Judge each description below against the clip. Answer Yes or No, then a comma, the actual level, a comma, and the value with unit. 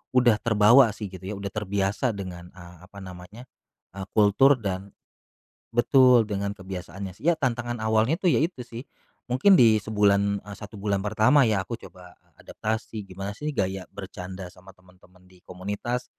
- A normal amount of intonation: Yes, average, 3.7 semitones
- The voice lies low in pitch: Yes, low, 100 Hz